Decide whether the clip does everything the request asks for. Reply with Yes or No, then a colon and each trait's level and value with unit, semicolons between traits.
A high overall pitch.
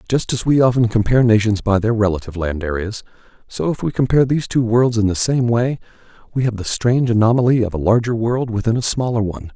No: low, 115 Hz